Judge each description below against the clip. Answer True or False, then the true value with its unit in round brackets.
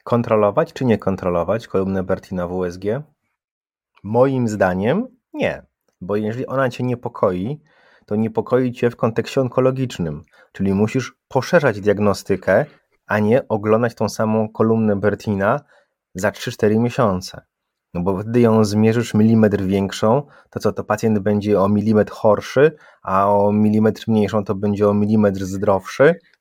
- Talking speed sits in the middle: True (135 wpm)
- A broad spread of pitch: False (2.8 semitones)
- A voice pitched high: False (105 Hz)